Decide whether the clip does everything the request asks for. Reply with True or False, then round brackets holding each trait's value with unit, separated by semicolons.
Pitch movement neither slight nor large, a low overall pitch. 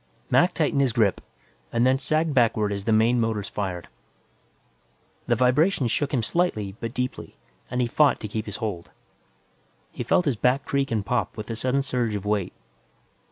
True (4.2 semitones; 120 Hz)